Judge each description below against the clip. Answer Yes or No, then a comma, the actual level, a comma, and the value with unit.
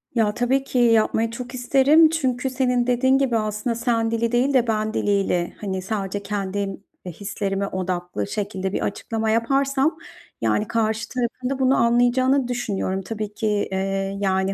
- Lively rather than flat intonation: No, average, 4.0 semitones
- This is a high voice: Yes, high, 225 Hz